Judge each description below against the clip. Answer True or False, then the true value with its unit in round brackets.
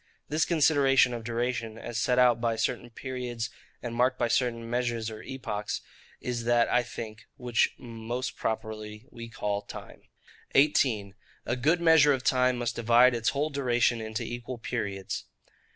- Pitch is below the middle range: True (120 Hz)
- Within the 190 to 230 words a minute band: False (155 wpm)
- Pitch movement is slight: True (1.9 semitones)